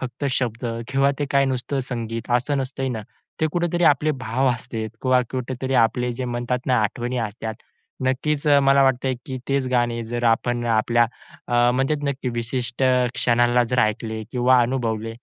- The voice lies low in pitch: Yes, low, 125 Hz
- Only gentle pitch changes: Yes, narrow, 2.1 semitones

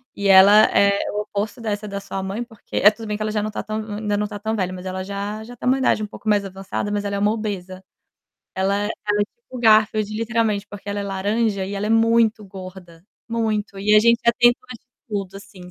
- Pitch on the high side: Yes, high, 210 Hz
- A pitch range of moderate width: No, narrow, 1.7 semitones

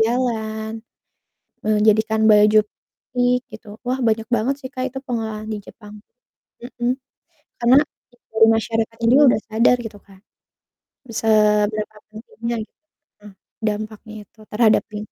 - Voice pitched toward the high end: Yes, high, 220 Hz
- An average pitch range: No, narrow, 1.6 semitones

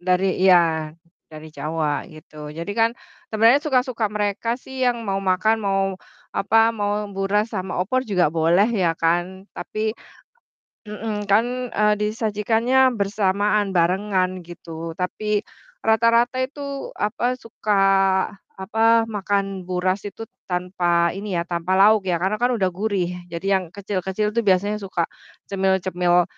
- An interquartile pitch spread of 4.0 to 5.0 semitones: No, average, 3.3 semitones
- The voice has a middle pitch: No, high, 195 Hz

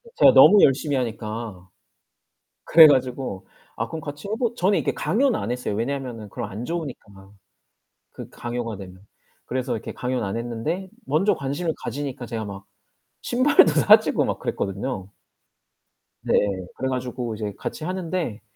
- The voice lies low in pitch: Yes, low, 125 Hz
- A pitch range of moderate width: No, wide, 6.3 semitones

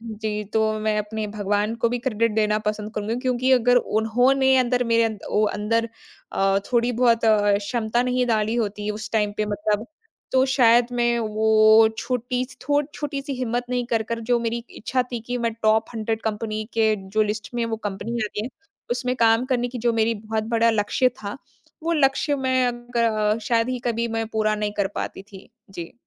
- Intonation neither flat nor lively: No, narrow, 2.3 semitones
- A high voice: Yes, high, 225 Hz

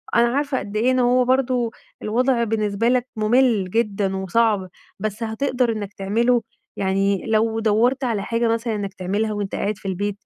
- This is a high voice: Yes, high, 220 Hz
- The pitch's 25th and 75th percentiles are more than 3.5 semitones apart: No, average, 3.0 semitones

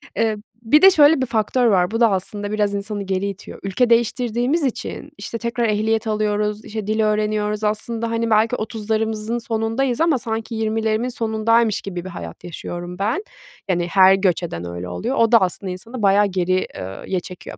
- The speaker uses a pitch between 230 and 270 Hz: No, high, 215 Hz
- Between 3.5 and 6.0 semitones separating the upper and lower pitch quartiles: No, average, 2.8 semitones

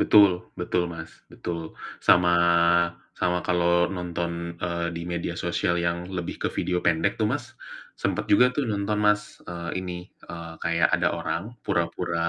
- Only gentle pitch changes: Yes, narrow, 0.9 semitones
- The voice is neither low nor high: No, very low, 85 Hz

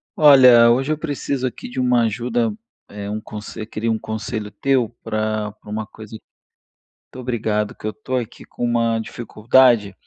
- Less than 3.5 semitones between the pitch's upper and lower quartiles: Yes, average, 2.8 semitones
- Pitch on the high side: No, low, 115 Hz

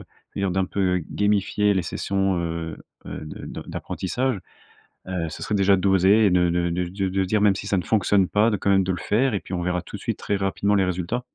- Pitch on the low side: Yes, very low, 95 Hz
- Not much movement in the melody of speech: Yes, narrow, 2.2 semitones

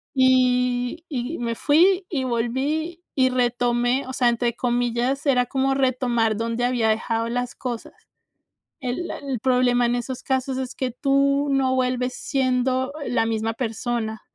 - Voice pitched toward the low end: No, very high, 250 Hz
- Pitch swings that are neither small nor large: No, narrow, 1.7 semitones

